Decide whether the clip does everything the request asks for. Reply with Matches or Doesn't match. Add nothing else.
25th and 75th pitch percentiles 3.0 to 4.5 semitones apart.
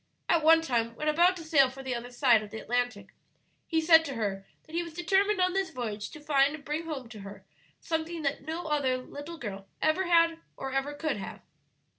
Doesn't match